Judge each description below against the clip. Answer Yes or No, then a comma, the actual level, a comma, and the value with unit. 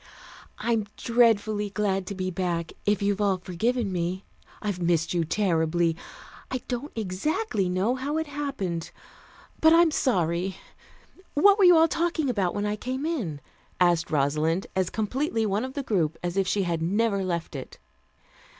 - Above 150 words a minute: Yes, average, 160 wpm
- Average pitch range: No, wide, 6.1 semitones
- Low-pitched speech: No, high, 200 Hz